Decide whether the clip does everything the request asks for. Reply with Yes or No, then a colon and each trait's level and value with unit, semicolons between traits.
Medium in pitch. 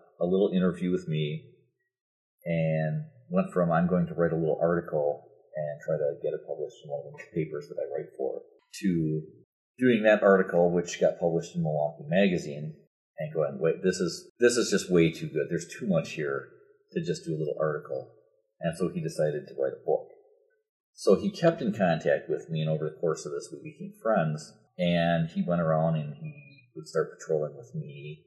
No: low, 120 Hz